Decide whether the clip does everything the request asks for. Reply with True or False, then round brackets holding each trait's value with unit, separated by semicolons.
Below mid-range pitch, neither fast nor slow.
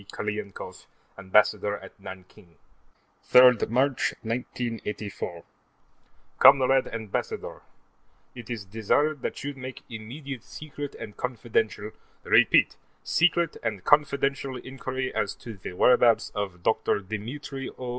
False (120 Hz; 105 wpm)